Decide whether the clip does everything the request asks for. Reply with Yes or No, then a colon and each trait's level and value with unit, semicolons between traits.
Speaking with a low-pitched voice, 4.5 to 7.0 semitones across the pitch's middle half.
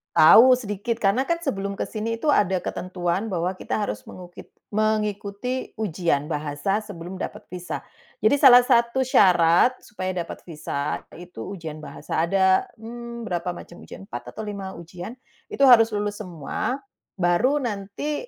No: high, 200 Hz; average, 4.8 semitones